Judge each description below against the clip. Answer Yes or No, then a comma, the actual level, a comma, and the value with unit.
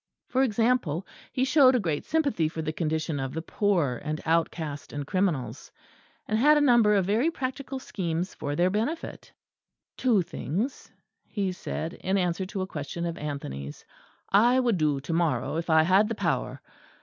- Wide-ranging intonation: Yes, wide, 6.6 semitones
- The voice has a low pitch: No, medium, 185 Hz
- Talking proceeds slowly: No, average, 175 wpm